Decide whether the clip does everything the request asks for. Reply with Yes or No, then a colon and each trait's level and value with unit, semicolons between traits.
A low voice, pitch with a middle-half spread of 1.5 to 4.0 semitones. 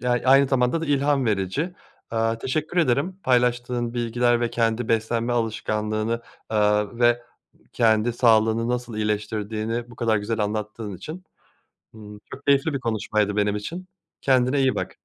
Yes: low, 115 Hz; average, 2.7 semitones